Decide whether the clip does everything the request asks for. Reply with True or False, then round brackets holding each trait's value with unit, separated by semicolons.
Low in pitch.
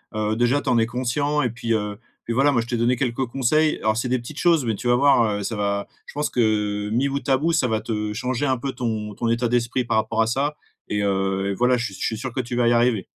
True (120 Hz)